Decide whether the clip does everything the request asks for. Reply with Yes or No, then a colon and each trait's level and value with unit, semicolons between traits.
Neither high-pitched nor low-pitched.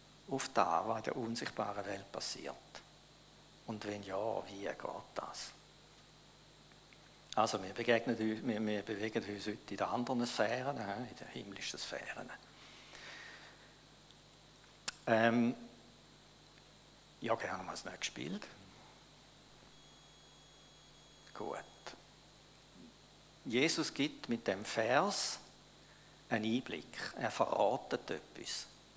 No: low, 115 Hz